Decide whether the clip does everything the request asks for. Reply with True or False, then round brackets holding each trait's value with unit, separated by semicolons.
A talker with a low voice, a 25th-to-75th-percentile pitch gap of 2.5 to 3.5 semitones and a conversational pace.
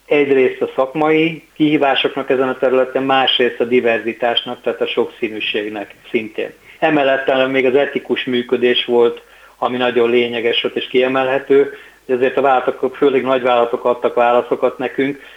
True (130 Hz; 3.2 semitones; 135 wpm)